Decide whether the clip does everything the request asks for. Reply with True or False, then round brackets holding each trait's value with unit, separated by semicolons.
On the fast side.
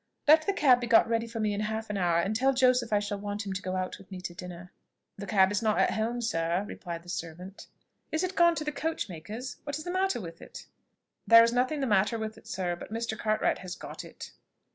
True (255 wpm)